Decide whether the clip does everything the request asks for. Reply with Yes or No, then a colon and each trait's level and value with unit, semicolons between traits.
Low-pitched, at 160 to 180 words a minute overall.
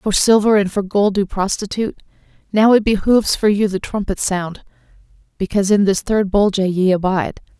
No: high, 200 Hz; average, 175 wpm